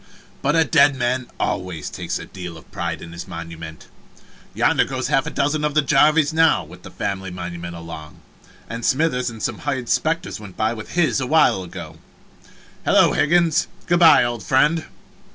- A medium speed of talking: Yes, average, 175 wpm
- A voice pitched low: Yes, low, 120 Hz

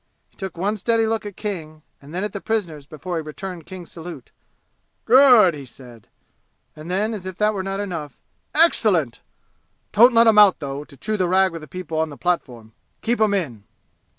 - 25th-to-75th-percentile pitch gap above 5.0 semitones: Yes, wide, 5.4 semitones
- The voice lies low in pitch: No, medium, 185 Hz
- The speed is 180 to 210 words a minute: Yes, average, 195 wpm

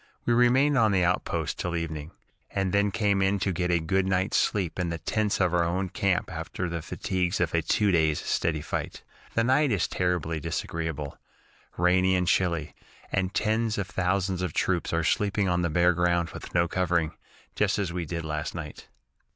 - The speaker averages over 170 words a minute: Yes, average, 190 wpm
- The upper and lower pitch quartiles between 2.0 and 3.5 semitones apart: Yes, average, 2.7 semitones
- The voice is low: Yes, very low, 90 Hz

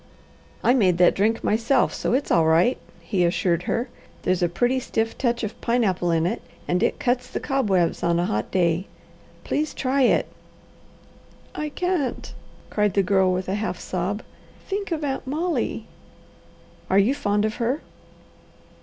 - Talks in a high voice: Yes, high, 210 Hz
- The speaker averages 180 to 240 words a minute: No, average, 165 wpm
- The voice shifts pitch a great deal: Yes, wide, 6.2 semitones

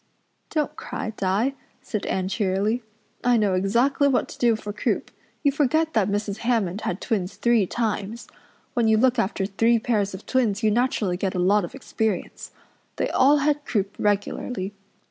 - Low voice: No, high, 220 Hz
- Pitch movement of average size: Yes, average, 3.8 semitones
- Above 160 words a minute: Yes, average, 170 wpm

